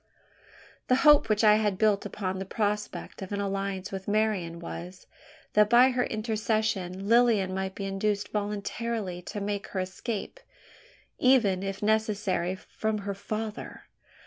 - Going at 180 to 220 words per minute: No, average, 145 wpm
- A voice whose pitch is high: Yes, high, 205 Hz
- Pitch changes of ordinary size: No, narrow, 2.2 semitones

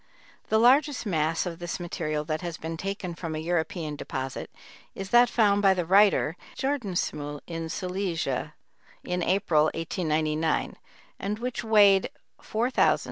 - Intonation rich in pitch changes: No, average, 4.2 semitones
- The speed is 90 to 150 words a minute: Yes, average, 145 wpm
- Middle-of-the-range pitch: Yes, medium, 175 Hz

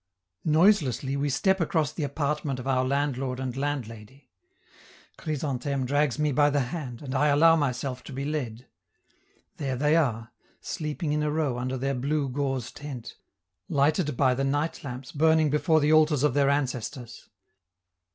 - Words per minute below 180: Yes, average, 160 wpm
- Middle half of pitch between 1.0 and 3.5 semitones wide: Yes, average, 2.8 semitones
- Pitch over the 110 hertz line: Yes, medium, 140 Hz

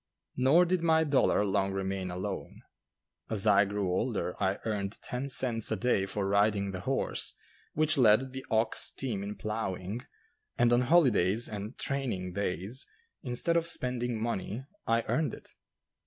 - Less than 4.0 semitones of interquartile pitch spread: No, average, 4.7 semitones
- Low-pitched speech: Yes, low, 110 Hz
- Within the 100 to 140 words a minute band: No, average, 155 wpm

